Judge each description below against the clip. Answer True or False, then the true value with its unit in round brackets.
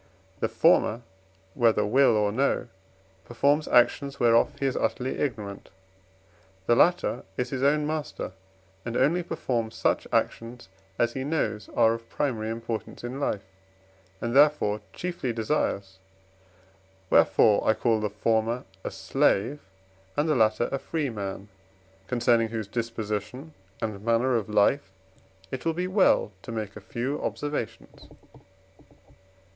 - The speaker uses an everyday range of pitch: True (4.2 semitones)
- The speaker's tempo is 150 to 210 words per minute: False (135 wpm)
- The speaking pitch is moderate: False (120 Hz)